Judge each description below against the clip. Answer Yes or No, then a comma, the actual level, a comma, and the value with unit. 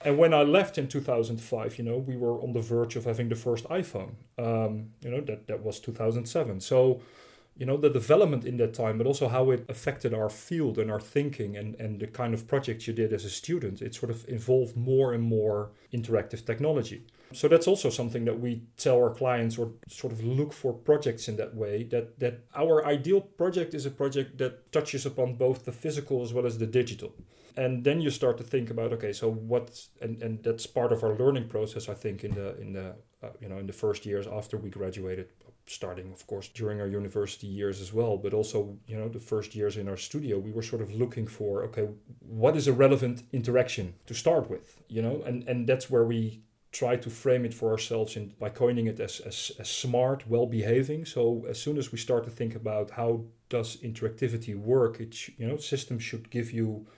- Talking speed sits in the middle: No, fast, 225 wpm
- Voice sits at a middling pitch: No, low, 120 Hz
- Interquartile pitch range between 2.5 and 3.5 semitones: Yes, average, 2.9 semitones